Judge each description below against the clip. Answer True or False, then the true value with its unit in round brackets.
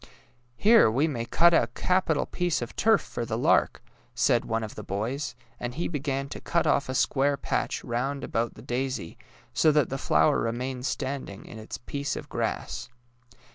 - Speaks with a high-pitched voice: False (135 Hz)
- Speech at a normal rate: True (185 wpm)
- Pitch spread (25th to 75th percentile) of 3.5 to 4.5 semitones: True (4.0 semitones)